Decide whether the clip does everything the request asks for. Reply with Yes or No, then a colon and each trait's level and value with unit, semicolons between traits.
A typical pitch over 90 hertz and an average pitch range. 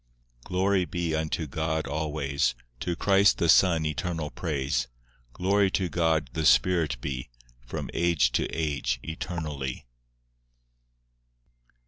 No: very low, 80 Hz; average, 3.5 semitones